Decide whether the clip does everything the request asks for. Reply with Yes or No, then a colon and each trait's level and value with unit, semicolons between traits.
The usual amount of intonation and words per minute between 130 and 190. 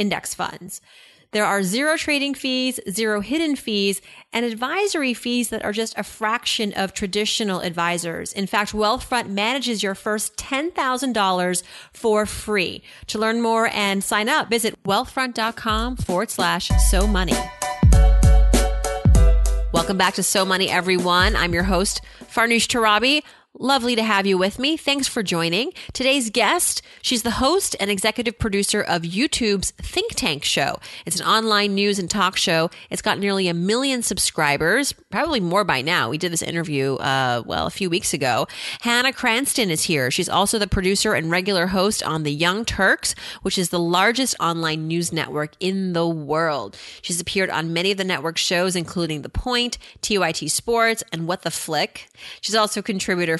Yes: average, 4.6 semitones; average, 165 wpm